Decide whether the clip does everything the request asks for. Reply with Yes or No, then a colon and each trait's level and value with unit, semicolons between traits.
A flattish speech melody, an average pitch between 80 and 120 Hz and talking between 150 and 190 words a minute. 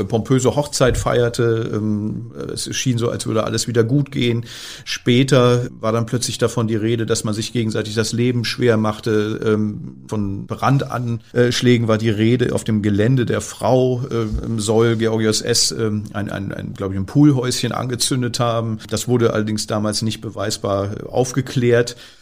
Yes: narrow, 2.1 semitones; low, 115 Hz; average, 155 wpm